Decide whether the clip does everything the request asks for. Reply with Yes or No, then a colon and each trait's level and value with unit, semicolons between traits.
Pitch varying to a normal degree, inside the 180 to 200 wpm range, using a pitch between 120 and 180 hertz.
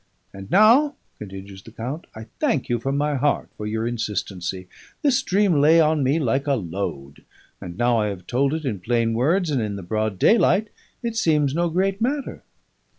No: wide, 7.9 semitones; average, 190 wpm; low, 135 Hz